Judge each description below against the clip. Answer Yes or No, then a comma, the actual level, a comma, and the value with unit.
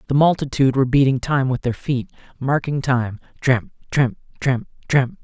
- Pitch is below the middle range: Yes, low, 130 Hz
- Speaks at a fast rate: No, average, 150 wpm